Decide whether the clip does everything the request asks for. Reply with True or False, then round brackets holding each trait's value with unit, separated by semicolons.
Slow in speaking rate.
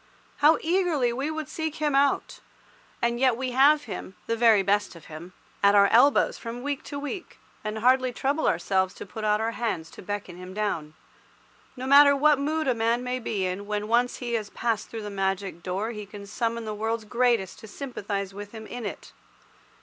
False (195 wpm)